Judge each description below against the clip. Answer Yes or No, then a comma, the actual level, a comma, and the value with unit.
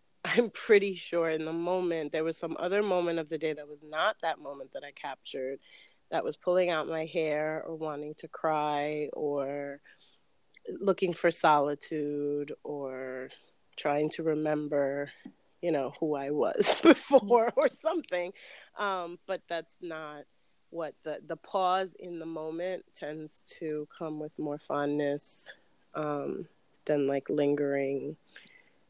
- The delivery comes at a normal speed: Yes, average, 145 wpm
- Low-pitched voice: No, medium, 155 Hz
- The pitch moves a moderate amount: Yes, average, 3.3 semitones